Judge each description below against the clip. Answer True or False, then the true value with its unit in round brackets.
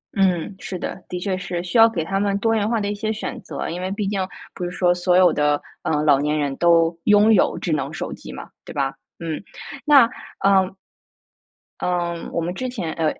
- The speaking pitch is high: False (180 Hz)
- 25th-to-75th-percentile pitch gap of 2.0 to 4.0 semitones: True (3.4 semitones)